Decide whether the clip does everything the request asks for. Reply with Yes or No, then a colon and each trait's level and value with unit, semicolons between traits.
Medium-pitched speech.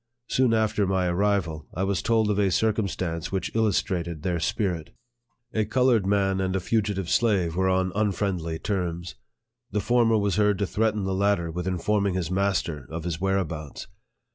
No: very low, 95 Hz